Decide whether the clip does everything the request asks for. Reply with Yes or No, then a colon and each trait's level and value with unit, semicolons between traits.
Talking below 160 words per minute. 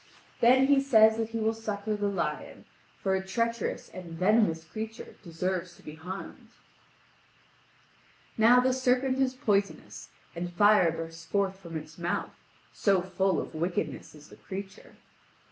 Yes: average, 145 wpm